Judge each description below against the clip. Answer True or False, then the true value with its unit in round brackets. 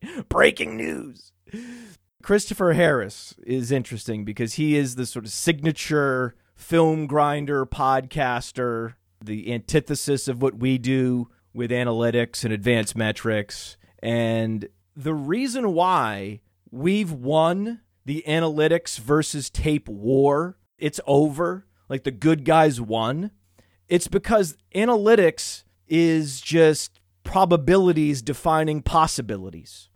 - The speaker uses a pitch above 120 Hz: True (135 Hz)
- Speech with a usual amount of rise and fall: False (5.9 semitones)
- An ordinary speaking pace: False (105 wpm)